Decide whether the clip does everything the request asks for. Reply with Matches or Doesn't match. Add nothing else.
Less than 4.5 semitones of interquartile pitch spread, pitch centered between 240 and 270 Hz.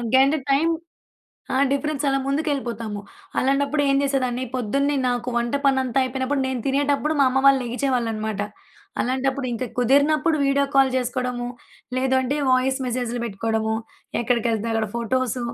Matches